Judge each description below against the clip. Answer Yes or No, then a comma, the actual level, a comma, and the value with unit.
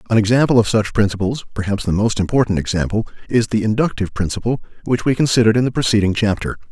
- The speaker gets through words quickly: No, average, 180 wpm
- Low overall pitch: Yes, low, 110 Hz